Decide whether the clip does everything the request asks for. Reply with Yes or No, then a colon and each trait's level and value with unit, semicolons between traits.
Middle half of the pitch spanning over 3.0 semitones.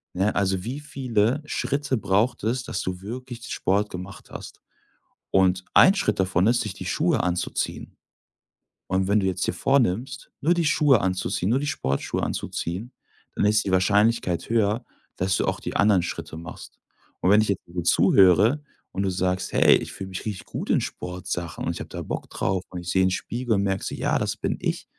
Yes: average, 4.6 semitones